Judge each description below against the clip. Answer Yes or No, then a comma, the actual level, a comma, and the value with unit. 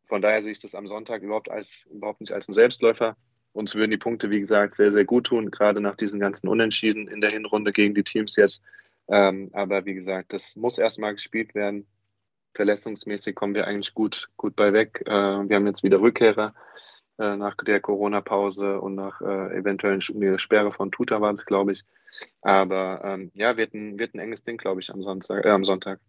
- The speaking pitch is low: Yes, low, 105 Hz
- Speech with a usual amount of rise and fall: No, narrow, 1.4 semitones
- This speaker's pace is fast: Yes, fast, 200 wpm